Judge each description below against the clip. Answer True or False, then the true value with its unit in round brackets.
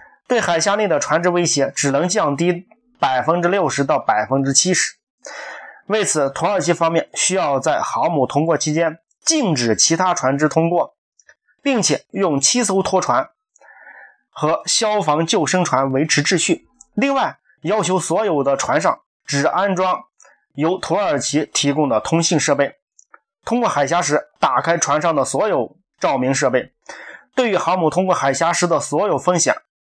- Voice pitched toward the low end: False (170 Hz)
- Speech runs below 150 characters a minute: False (235 characters per minute)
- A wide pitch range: True (6.1 semitones)